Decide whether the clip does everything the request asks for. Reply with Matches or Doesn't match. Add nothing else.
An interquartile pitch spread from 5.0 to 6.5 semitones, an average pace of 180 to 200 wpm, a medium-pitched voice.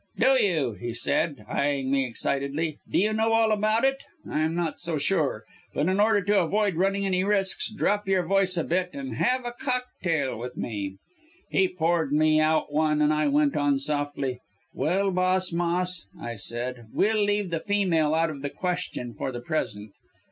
Matches